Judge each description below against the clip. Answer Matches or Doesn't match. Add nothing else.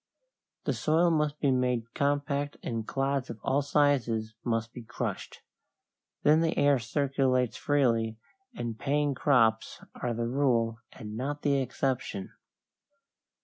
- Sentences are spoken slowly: Matches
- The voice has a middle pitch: Doesn't match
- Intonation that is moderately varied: Matches